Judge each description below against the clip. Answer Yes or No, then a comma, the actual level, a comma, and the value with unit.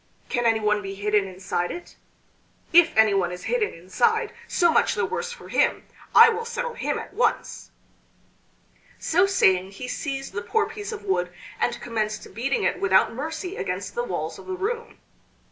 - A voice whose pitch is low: No, very high, 270 Hz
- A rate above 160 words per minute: Yes, average, 170 wpm